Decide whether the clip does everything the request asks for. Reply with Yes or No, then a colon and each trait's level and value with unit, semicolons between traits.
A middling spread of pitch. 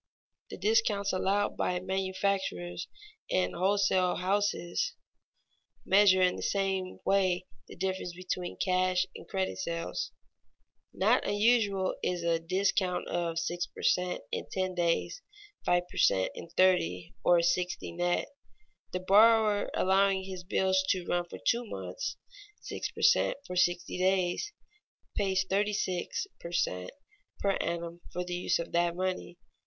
No: narrow, 1.8 semitones